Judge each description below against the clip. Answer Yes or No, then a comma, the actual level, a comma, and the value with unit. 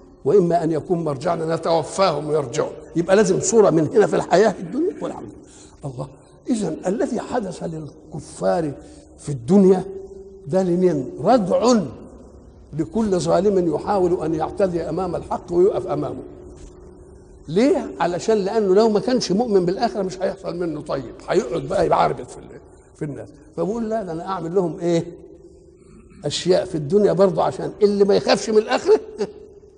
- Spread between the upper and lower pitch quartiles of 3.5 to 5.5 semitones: Yes, average, 4.4 semitones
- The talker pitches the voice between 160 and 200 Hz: Yes, high, 190 Hz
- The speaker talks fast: Yes, fast, 140 wpm